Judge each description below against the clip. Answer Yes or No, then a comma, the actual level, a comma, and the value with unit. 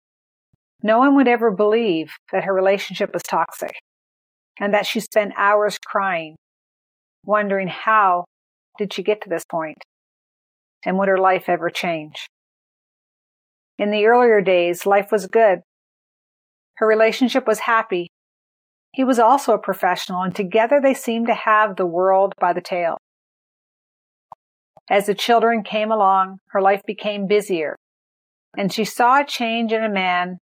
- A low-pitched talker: No, high, 205 Hz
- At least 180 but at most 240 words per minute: No, average, 145 wpm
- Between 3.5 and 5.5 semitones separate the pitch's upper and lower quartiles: No, average, 2.9 semitones